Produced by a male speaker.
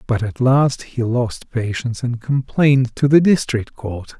Yes: male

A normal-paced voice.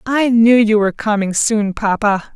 Yes: average, 180 wpm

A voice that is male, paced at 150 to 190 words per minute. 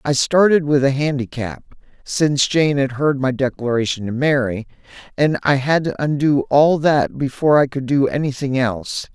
Yes: male; average, 170 wpm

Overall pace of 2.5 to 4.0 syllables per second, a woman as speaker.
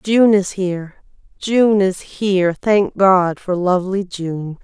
Yes: 3.6 syllables/s; female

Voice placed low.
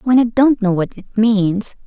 No: high, 215 Hz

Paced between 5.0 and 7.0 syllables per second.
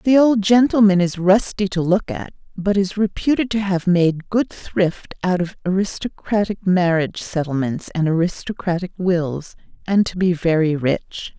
No: 4.4 syllables/s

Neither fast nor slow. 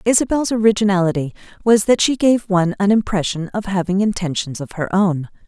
Yes: average, 165 wpm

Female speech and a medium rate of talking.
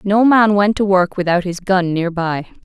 No: female; fast, 225 wpm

